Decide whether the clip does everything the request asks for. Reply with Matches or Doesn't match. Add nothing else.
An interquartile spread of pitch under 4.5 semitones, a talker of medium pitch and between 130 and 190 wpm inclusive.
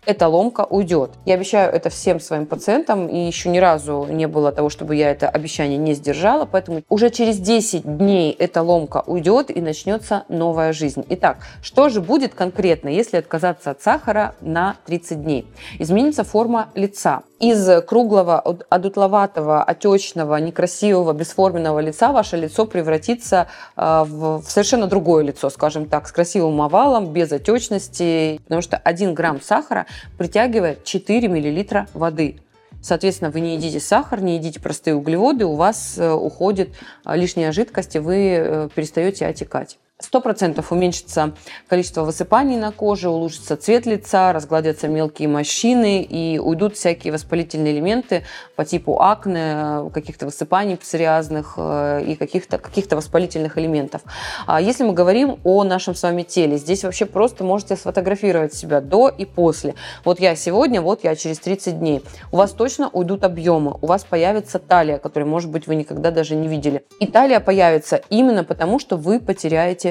Matches